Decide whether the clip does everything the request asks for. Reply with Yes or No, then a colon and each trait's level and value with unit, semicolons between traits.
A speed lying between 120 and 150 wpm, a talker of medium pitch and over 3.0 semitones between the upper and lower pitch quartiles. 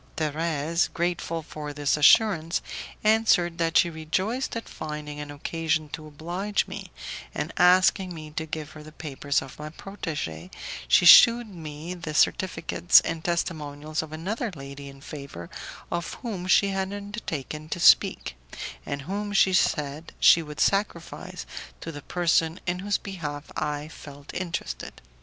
Yes: average, 145 wpm; medium, 160 Hz; average, 3.5 semitones